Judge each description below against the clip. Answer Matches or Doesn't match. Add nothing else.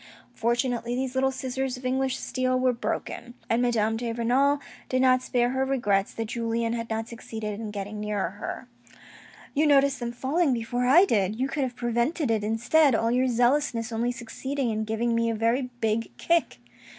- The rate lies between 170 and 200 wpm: Matches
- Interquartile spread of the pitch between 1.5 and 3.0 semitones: Matches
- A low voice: Doesn't match